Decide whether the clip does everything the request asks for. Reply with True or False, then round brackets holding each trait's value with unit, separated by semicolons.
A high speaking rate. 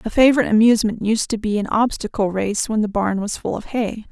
True (235 wpm)